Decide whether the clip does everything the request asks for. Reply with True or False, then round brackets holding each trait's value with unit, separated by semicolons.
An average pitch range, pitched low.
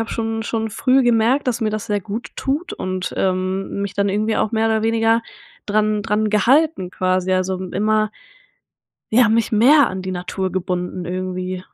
False (3.3 semitones; 210 Hz)